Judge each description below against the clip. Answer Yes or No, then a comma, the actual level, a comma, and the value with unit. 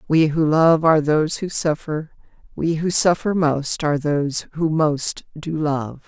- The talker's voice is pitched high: No, medium, 155 Hz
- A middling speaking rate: Yes, average, 170 wpm